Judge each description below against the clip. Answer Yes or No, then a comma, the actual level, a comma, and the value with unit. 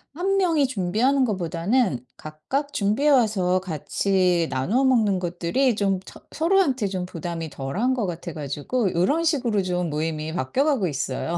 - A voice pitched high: Yes, high, 195 Hz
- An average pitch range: No, wide, 7.4 semitones